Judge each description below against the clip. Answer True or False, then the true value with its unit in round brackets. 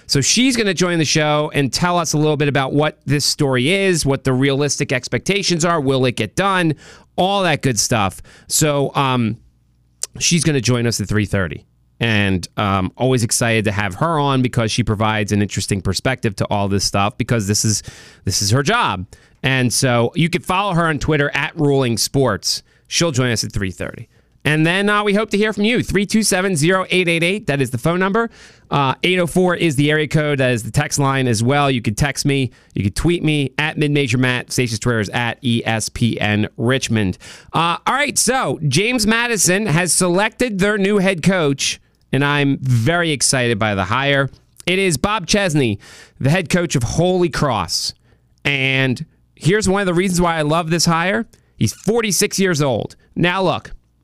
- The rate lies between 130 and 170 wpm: False (190 wpm)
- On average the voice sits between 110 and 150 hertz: True (140 Hz)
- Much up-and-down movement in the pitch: True (6.8 semitones)